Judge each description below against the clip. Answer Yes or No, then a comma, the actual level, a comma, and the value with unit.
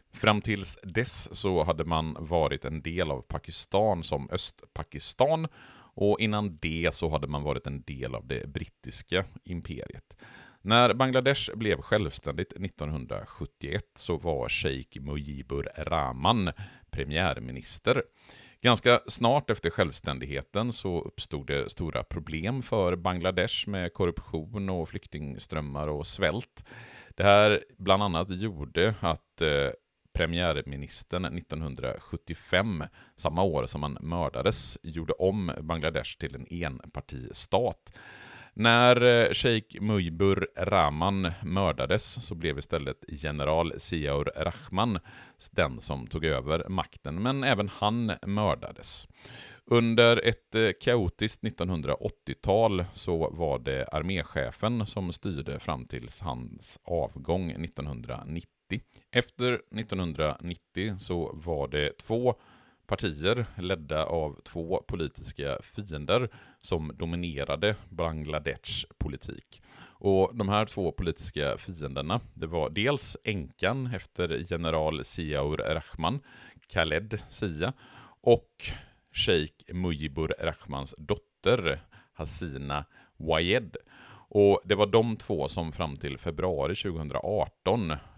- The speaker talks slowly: Yes, slow, 105 wpm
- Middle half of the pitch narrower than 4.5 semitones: No, average, 5.3 semitones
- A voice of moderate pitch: No, very low, 90 Hz